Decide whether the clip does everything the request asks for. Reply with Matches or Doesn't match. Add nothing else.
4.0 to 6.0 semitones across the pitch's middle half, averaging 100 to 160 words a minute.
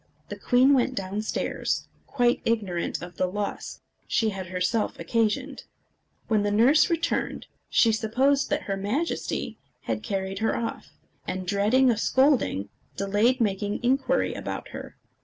Matches